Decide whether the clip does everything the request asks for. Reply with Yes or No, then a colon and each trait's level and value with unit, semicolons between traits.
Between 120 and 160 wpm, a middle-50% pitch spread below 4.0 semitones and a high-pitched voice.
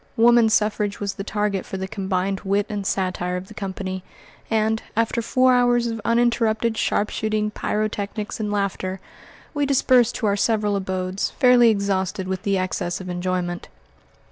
Yes: average, 155 wpm; average, 2.8 semitones; high, 205 Hz